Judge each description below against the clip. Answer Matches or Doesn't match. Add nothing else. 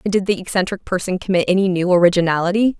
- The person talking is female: Matches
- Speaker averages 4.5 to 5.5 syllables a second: Doesn't match